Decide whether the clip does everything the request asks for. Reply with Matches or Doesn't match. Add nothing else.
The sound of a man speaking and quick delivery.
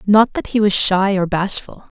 Doesn't match